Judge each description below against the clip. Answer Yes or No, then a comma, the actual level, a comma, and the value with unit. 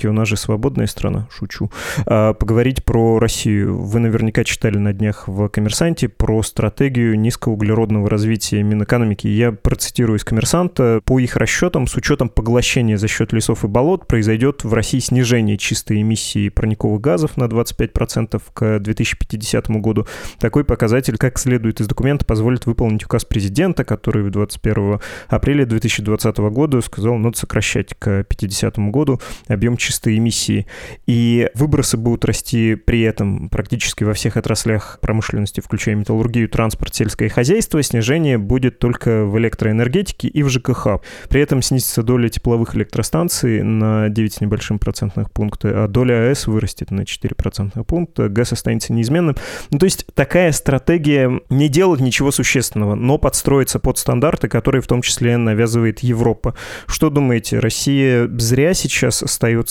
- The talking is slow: No, average, 145 wpm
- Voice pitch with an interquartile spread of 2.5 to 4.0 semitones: Yes, average, 3.1 semitones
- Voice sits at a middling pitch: No, low, 115 Hz